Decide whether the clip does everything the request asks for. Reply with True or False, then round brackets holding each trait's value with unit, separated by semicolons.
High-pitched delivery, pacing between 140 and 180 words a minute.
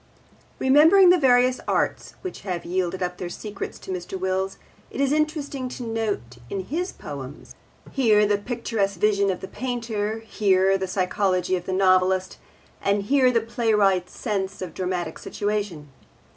True (200 Hz; 155 wpm)